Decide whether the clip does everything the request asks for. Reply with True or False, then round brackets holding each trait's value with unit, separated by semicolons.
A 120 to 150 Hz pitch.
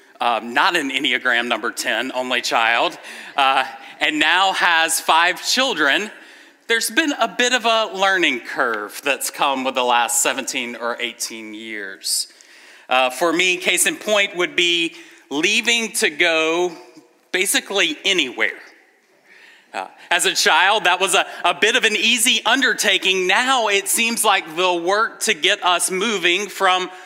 False (190 Hz)